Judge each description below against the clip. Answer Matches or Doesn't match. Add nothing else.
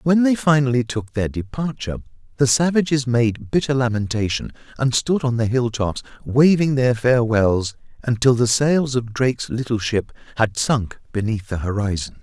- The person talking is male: Matches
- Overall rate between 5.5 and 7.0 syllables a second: Doesn't match